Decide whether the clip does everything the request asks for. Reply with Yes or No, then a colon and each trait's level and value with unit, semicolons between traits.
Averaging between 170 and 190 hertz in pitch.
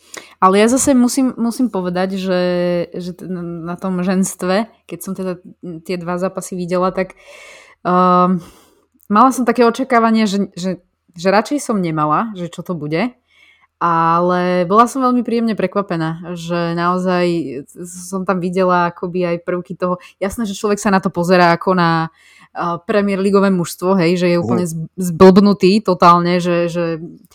Yes: medium, 185 Hz